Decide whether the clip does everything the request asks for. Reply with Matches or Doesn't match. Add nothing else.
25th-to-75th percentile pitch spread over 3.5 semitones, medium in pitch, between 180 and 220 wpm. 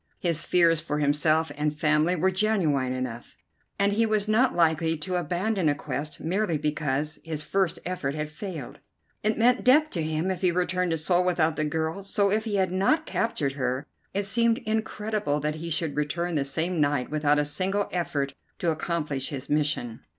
Matches